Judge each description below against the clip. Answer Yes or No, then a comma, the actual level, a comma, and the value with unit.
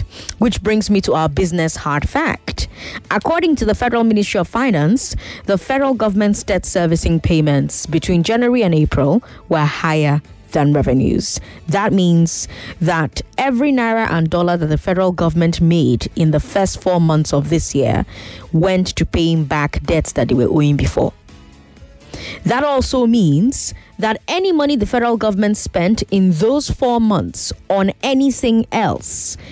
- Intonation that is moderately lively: No, wide, 6.6 semitones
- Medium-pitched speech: Yes, medium, 180 Hz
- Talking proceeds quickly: No, average, 155 wpm